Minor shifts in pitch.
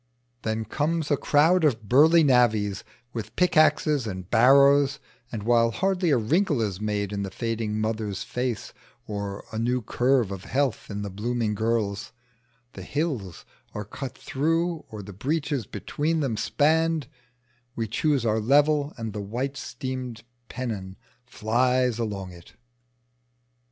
No: average, 5.3 semitones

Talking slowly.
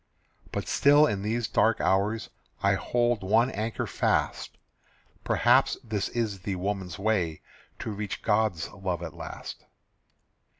Yes: slow, 130 wpm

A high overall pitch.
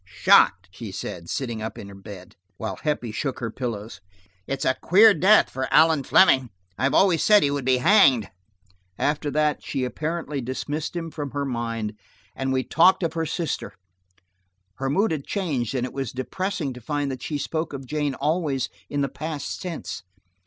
No: medium, 140 Hz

